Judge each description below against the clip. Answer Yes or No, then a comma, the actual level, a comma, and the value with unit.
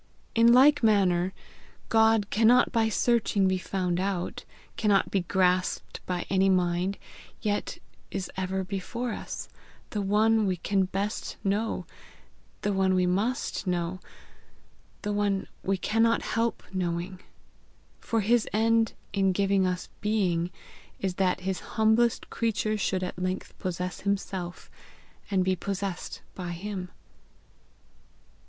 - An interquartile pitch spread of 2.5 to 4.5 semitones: Yes, average, 2.9 semitones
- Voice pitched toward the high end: Yes, high, 195 Hz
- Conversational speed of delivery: No, slow, 125 wpm